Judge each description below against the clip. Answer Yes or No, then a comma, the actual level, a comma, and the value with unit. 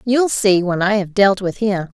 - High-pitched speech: Yes, high, 200 Hz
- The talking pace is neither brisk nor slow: No, fast, 240 wpm